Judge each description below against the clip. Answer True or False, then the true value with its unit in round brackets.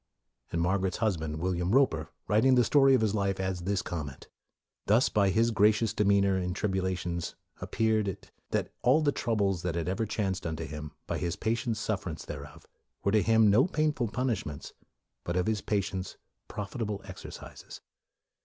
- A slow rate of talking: False (180 wpm)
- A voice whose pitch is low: True (100 Hz)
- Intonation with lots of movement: False (3.8 semitones)